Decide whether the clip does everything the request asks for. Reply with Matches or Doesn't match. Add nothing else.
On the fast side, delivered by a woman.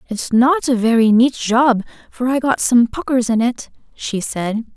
Doesn't match